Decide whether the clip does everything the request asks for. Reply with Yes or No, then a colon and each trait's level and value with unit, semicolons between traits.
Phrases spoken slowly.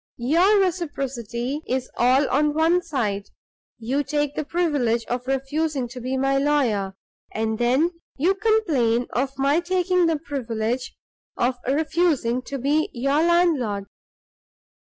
Yes: slow, 130 wpm